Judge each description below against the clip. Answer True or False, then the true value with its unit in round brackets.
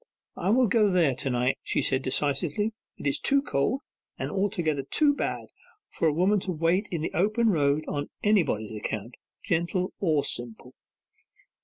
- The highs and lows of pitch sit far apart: True (6.5 semitones)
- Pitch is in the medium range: True (165 Hz)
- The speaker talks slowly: False (165 wpm)